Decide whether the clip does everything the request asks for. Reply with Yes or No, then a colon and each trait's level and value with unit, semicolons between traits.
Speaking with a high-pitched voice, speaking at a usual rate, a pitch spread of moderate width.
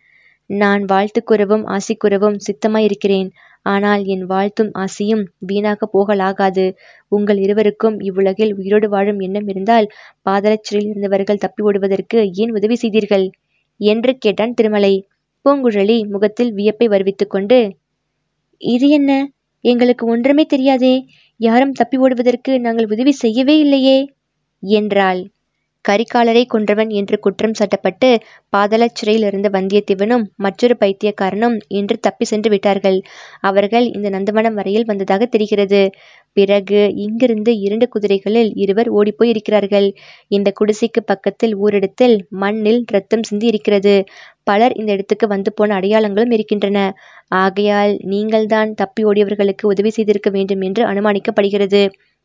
No: high, 210 Hz; average, 110 wpm; narrow, 2.3 semitones